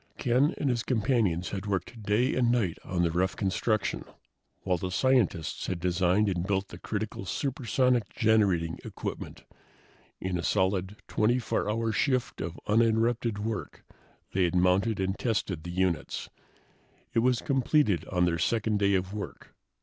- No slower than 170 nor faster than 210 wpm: No, average, 150 wpm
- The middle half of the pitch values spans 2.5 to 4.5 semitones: Yes, average, 4.1 semitones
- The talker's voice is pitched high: No, low, 105 Hz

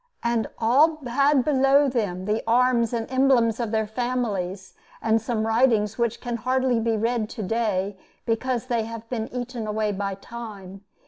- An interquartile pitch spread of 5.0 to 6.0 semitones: No, narrow, 2.5 semitones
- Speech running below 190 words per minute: Yes, average, 165 wpm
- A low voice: No, high, 230 Hz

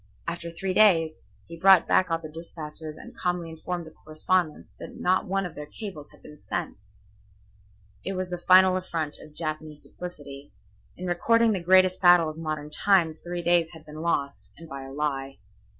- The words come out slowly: No, average, 180 wpm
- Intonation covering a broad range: No, average, 2.9 semitones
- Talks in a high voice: No, medium, 165 Hz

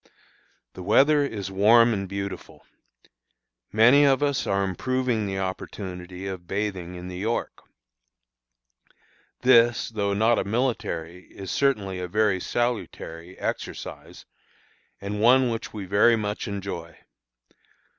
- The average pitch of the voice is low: Yes, low, 100 Hz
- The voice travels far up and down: No, average, 3.9 semitones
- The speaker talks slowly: Yes, slow, 120 wpm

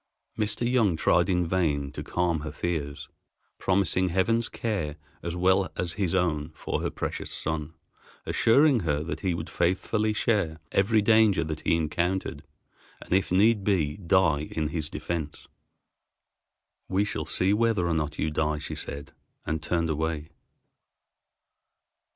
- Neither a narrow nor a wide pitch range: Yes, average, 4.0 semitones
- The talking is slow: No, average, 145 wpm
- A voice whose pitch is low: Yes, very low, 85 Hz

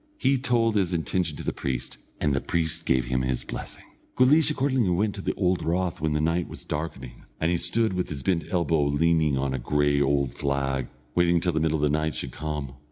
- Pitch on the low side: Yes, very low, 80 Hz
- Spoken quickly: Yes, fast, 225 wpm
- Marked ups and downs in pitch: No, average, 4.3 semitones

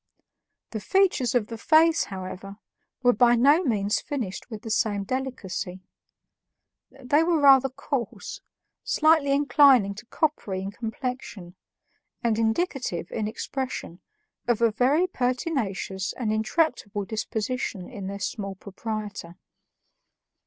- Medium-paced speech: No, slow, 115 wpm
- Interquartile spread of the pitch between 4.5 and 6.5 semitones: Yes, average, 5.1 semitones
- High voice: Yes, high, 230 Hz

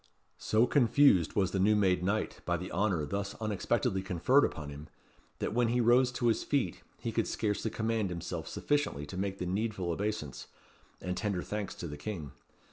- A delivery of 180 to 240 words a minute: Yes, average, 185 wpm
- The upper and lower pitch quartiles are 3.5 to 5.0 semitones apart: Yes, average, 3.9 semitones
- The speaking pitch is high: No, low, 100 Hz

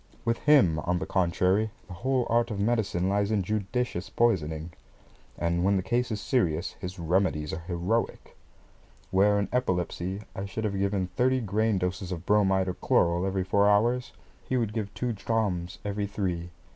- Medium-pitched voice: No, low, 100 Hz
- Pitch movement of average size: Yes, average, 3.5 semitones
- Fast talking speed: No, average, 170 wpm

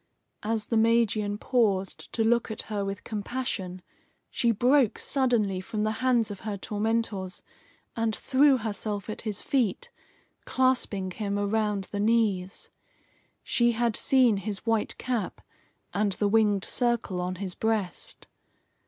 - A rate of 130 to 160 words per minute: Yes, slow, 135 wpm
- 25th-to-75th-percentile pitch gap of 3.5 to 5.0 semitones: No, narrow, 2.6 semitones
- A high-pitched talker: Yes, high, 215 Hz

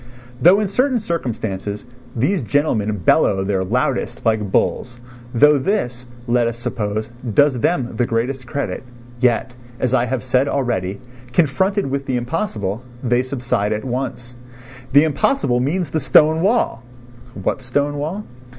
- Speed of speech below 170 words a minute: Yes, average, 140 wpm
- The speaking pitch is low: Yes, low, 125 Hz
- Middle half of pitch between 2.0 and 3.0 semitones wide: No, average, 4.0 semitones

